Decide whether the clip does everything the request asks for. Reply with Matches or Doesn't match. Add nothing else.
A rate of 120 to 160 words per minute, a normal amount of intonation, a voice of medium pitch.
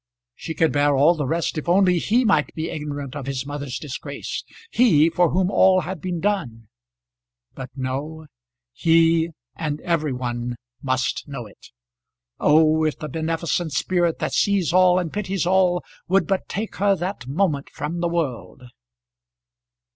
Matches